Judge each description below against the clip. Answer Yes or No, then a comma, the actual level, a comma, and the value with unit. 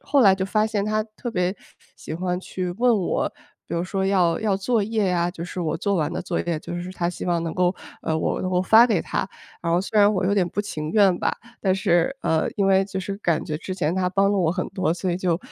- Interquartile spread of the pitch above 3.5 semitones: No, narrow, 2.5 semitones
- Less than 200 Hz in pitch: Yes, medium, 185 Hz